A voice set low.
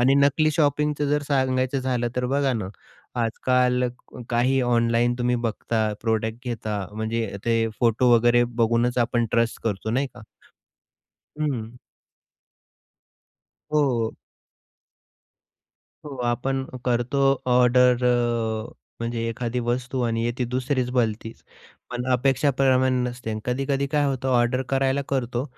Yes: low, 125 Hz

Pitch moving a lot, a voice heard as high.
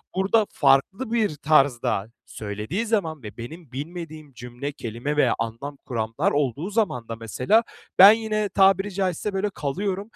No: wide, 8.1 semitones; medium, 155 Hz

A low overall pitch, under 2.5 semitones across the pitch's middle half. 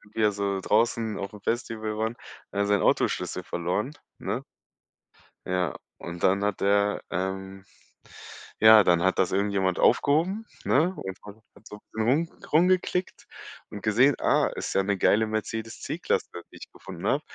No: low, 105 Hz; average, 2.8 semitones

